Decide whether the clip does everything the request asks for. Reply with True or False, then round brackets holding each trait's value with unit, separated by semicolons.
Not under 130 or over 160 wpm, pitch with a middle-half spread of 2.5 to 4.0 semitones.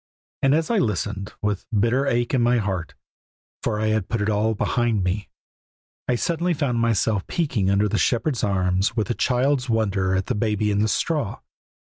False (190 wpm; 3.4 semitones)